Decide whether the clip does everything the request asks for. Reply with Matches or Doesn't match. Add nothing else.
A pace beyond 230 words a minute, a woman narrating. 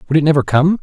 Doesn't match